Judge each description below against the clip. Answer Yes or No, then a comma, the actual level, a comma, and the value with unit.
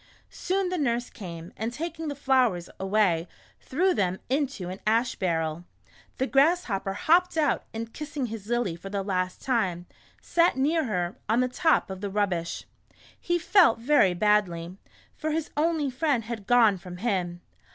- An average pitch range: No, wide, 7.6 semitones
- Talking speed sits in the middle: Yes, average, 165 wpm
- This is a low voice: No, high, 230 Hz